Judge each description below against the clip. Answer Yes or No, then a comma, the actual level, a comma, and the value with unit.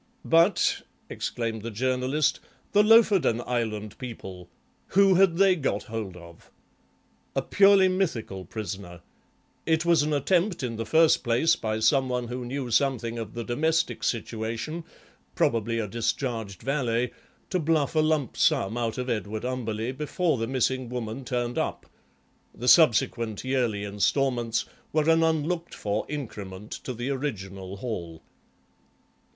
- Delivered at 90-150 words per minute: Yes, average, 140 wpm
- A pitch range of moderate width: No, wide, 5.7 semitones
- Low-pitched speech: Yes, low, 125 Hz